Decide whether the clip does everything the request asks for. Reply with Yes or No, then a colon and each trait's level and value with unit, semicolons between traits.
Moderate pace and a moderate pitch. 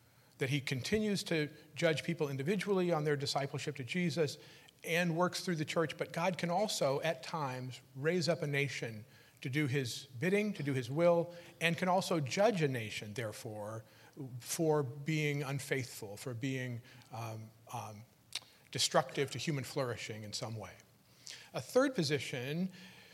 Yes: average, 155 wpm; medium, 145 Hz